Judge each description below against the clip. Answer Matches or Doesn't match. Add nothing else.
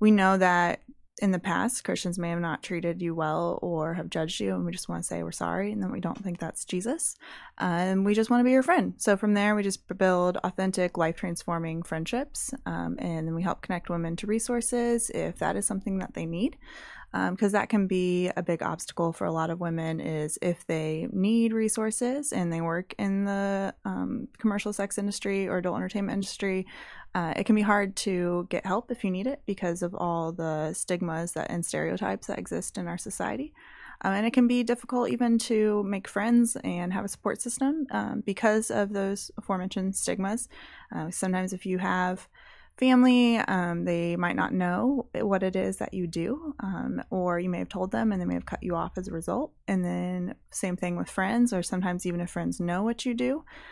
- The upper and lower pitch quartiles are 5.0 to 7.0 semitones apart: Doesn't match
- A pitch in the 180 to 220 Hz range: Matches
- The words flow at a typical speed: Doesn't match